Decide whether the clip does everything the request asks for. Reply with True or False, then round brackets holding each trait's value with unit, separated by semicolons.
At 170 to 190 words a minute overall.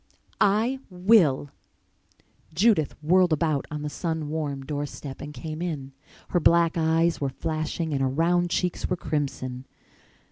False (145 wpm)